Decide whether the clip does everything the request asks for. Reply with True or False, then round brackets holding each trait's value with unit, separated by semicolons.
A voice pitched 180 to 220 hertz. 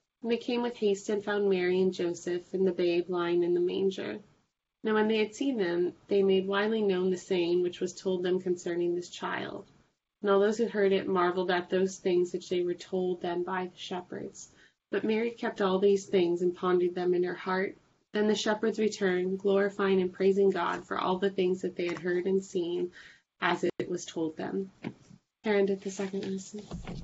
True (185 Hz)